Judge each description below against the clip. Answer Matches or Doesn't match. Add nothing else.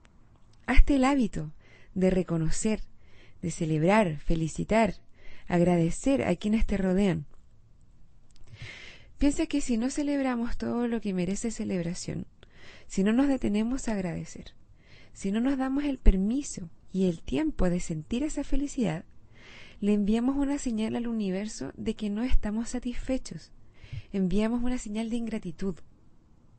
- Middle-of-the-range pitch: Doesn't match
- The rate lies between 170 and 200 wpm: Doesn't match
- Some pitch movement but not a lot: Doesn't match